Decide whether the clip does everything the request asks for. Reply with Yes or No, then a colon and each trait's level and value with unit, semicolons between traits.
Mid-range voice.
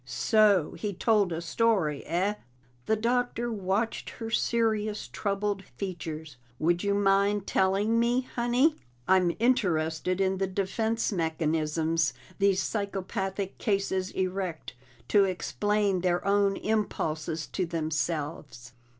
No: high, 195 Hz